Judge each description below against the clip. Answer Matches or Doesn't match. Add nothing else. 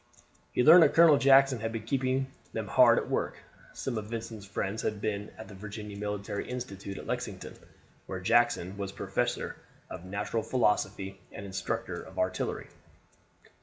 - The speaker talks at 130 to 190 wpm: Matches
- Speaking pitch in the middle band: Doesn't match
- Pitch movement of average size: Matches